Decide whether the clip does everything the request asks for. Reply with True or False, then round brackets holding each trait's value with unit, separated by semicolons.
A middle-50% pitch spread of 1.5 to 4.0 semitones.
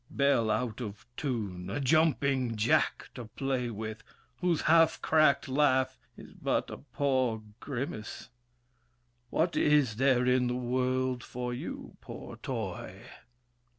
True (3.0 semitones)